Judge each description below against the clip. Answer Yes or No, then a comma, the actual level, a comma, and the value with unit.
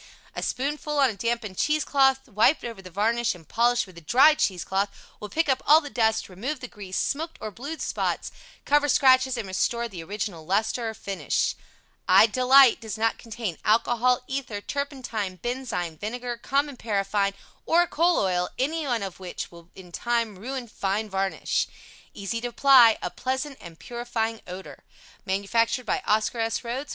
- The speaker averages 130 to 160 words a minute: No, average, 175 wpm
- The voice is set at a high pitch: Yes, high, 230 Hz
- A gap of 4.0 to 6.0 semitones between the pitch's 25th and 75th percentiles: Yes, average, 4.9 semitones